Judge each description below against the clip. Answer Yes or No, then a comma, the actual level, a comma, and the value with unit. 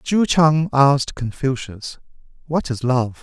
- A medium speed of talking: No, slow, 130 wpm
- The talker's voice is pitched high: No, medium, 140 Hz